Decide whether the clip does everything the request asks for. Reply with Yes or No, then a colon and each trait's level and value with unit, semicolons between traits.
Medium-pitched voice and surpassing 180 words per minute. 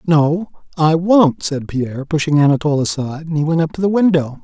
Yes: medium, 160 Hz; fast, 205 wpm